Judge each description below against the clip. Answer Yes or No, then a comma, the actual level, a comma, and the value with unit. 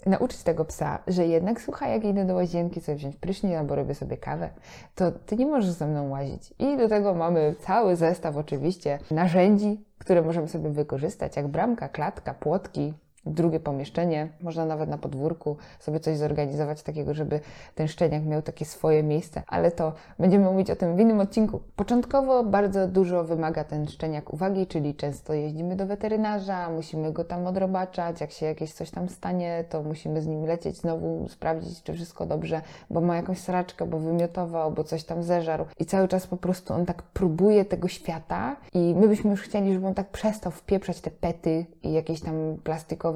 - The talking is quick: Yes, fast, 185 wpm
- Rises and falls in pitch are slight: No, average, 3.3 semitones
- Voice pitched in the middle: Yes, medium, 170 Hz